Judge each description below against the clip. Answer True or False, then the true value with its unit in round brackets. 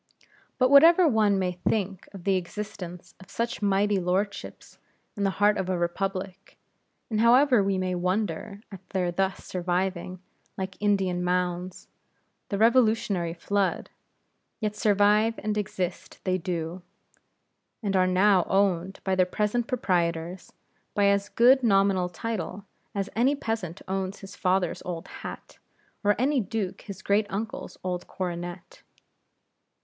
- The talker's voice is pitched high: True (195 Hz)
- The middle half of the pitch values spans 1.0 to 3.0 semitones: True (2.5 semitones)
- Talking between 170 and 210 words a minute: False (135 wpm)